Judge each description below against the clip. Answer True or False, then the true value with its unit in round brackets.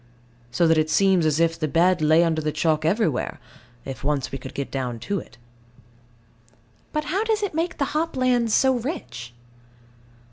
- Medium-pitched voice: True (165 Hz)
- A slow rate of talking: False (180 wpm)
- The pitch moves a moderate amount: False (9.0 semitones)